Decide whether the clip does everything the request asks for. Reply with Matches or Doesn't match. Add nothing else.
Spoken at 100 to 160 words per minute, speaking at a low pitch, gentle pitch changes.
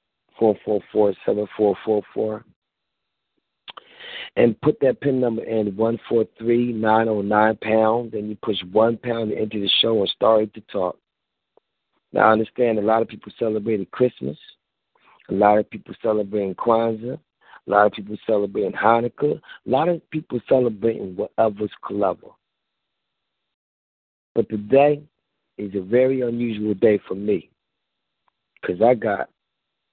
Matches